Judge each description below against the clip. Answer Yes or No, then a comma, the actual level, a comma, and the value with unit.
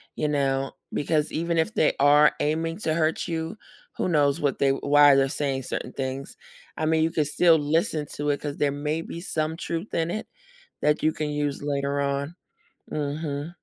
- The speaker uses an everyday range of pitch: No, narrow, 2.2 semitones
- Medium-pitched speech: Yes, medium, 150 Hz